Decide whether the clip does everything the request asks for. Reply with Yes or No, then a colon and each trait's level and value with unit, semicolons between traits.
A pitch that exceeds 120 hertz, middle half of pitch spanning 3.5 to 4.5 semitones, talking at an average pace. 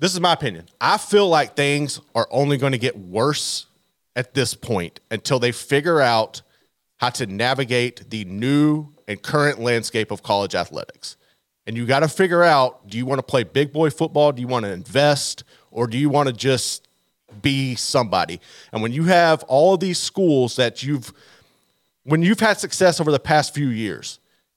Yes: low, 135 Hz; average, 3.9 semitones; average, 190 wpm